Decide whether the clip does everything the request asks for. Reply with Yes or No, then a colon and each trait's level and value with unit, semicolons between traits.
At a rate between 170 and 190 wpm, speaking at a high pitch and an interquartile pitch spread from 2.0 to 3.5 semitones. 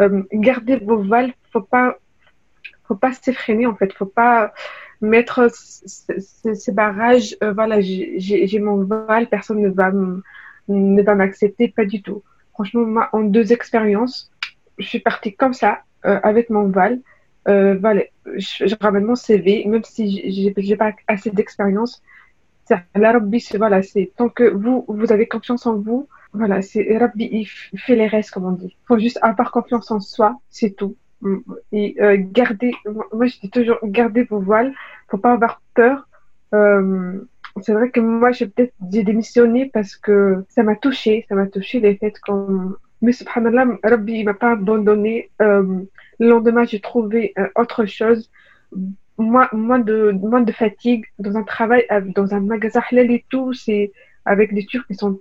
Yes: average, 180 wpm; high, 220 Hz; average, 2.7 semitones